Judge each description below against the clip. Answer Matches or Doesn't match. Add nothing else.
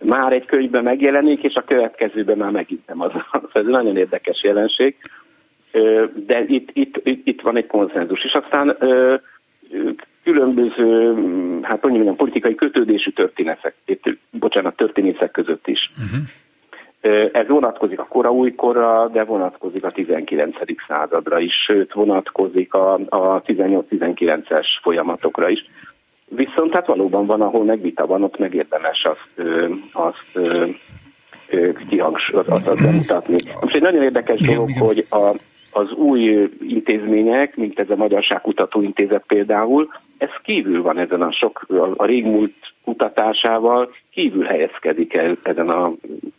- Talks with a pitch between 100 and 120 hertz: Doesn't match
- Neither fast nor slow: Matches